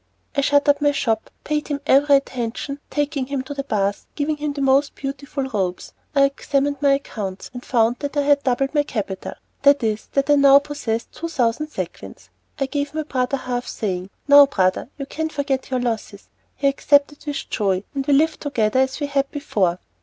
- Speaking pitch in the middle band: No, very high, 275 Hz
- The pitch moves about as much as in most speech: Yes, average, 3.6 semitones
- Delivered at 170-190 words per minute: No, average, 200 wpm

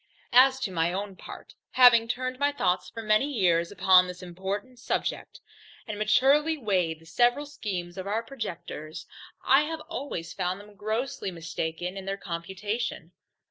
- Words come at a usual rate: Yes, average, 155 wpm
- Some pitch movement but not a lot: No, wide, 5.9 semitones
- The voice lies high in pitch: Yes, high, 205 Hz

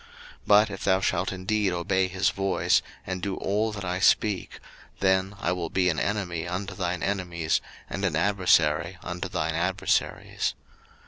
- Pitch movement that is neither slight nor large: No, narrow, 2.0 semitones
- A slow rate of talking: No, average, 165 wpm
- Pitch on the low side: Yes, very low, 95 Hz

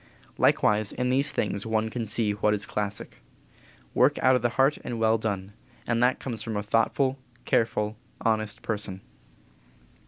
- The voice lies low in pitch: Yes, low, 110 Hz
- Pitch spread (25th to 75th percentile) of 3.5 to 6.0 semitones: No, narrow, 2.5 semitones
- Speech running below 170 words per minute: Yes, average, 160 wpm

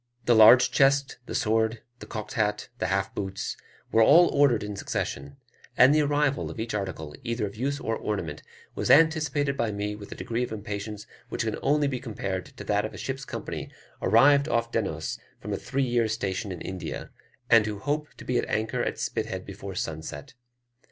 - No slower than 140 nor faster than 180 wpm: No, average, 195 wpm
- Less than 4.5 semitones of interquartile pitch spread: No, average, 4.9 semitones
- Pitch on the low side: Yes, low, 110 Hz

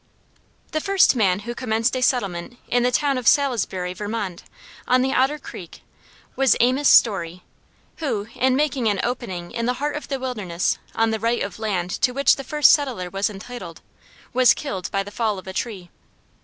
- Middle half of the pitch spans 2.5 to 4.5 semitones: No, average, 5.0 semitones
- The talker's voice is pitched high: Yes, high, 235 Hz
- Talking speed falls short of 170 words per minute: No, average, 185 wpm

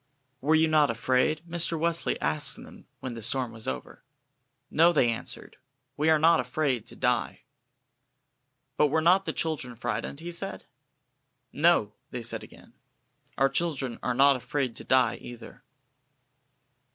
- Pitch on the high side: No, medium, 140 Hz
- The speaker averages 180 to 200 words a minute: No, average, 150 wpm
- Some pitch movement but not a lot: Yes, average, 4.5 semitones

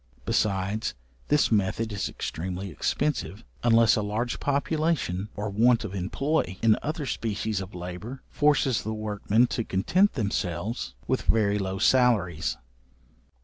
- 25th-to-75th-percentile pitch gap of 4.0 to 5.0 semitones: Yes, average, 4.3 semitones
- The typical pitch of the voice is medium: No, low, 110 Hz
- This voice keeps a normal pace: No, slow, 130 wpm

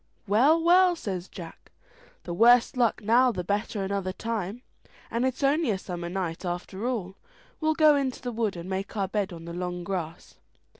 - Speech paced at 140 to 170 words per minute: No, average, 185 wpm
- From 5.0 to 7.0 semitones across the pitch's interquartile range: Yes, wide, 5.4 semitones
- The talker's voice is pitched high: Yes, high, 205 Hz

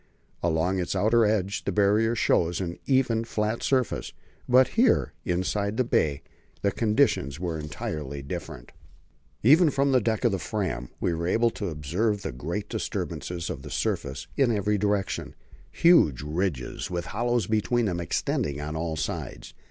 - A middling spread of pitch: No, wide, 5.7 semitones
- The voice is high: No, low, 100 Hz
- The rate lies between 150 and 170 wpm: Yes, average, 155 wpm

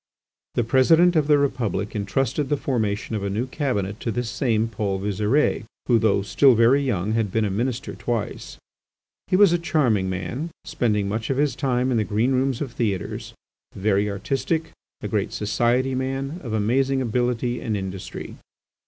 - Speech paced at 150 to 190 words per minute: Yes, average, 170 wpm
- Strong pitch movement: No, average, 4.3 semitones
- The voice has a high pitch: No, low, 120 Hz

